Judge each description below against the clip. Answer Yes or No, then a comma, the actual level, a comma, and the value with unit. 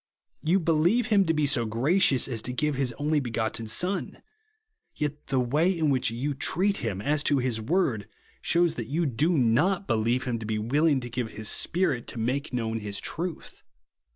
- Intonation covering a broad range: Yes, wide, 5.7 semitones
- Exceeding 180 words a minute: Yes, average, 190 wpm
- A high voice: No, low, 135 Hz